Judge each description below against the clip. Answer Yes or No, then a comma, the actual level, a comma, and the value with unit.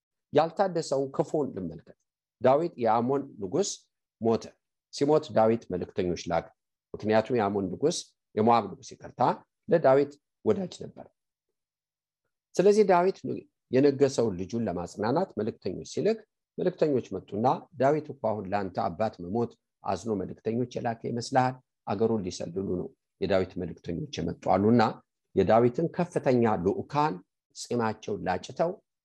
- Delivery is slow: Yes, slow, 105 wpm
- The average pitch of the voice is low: Yes, low, 130 Hz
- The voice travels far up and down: Yes, wide, 5.7 semitones